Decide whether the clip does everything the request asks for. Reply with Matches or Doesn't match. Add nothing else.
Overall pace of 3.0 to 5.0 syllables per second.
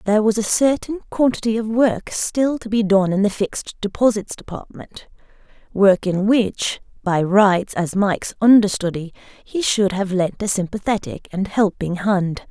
Matches